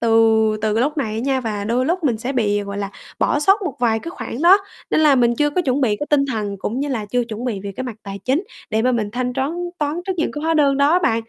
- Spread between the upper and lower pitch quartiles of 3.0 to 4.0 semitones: No, average, 5.0 semitones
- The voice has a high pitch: Yes, very high, 255 Hz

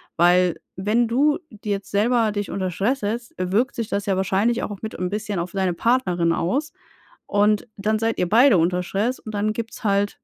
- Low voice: No, high, 205 Hz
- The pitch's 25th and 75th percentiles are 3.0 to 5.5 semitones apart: Yes, average, 3.5 semitones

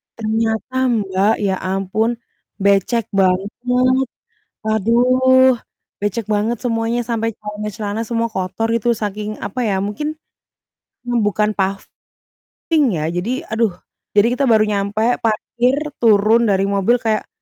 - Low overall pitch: No, high, 215 Hz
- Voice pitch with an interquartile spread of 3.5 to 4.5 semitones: No, average, 2.7 semitones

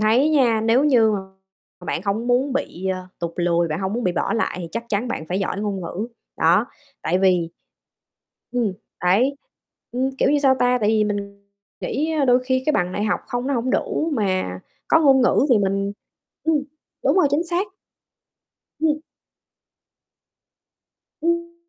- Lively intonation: Yes, wide, 5.9 semitones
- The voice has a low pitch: No, high, 230 Hz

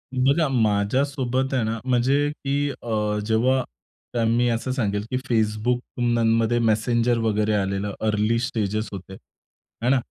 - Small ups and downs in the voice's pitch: No, average, 3.1 semitones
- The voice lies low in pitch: Yes, low, 115 Hz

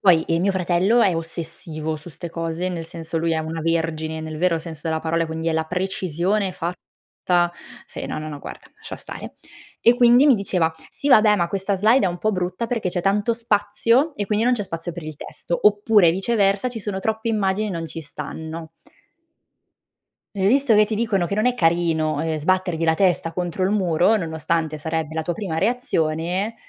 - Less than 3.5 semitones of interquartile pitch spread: No, average, 4.3 semitones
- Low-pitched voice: No, medium, 175 Hz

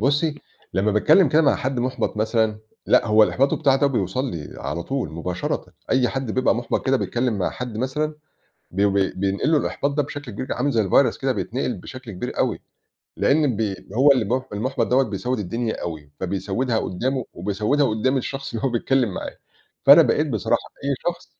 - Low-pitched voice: Yes, low, 125 Hz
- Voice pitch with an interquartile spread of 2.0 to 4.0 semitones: No, average, 4.8 semitones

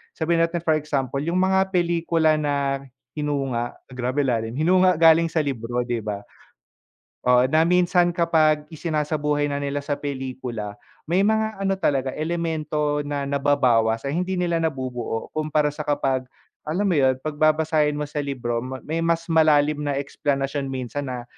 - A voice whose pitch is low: No, medium, 150 Hz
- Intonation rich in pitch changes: No, average, 3.3 semitones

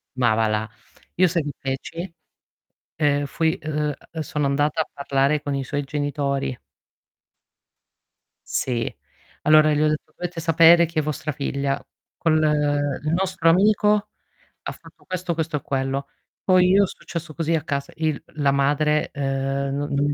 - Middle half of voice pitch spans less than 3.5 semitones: Yes, average, 2.8 semitones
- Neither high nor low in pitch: Yes, medium, 150 Hz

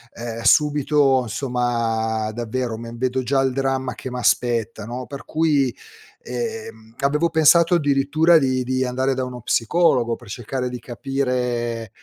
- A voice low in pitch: Yes, low, 130 Hz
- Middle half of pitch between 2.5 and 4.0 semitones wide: Yes, average, 2.8 semitones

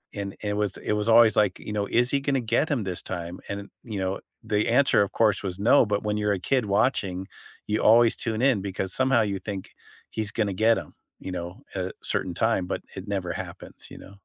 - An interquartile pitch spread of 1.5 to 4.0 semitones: Yes, average, 3.0 semitones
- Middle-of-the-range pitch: No, low, 105 Hz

